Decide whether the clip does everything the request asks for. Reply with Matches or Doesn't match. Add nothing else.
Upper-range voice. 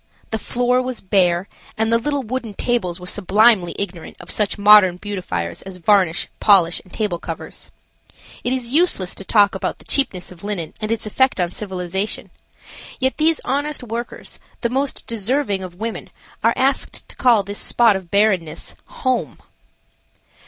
Matches